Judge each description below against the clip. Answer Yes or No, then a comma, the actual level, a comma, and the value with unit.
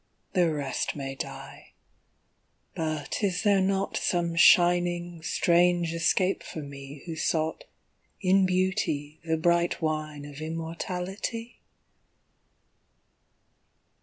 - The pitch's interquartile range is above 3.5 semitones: No, average, 2.8 semitones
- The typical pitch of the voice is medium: Yes, medium, 170 Hz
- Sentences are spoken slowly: Yes, slow, 100 wpm